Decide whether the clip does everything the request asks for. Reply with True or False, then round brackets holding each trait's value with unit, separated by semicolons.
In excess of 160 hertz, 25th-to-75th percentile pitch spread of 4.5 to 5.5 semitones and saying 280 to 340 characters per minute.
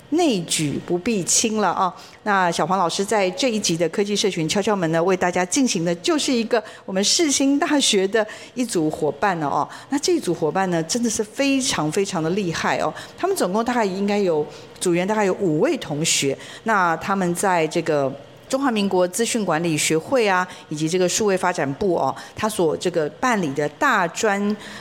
True (190 Hz; 5.1 semitones; 290 characters per minute)